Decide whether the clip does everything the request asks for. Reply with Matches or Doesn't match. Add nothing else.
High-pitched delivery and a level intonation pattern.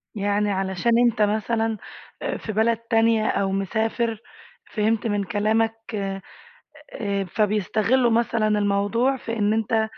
Matches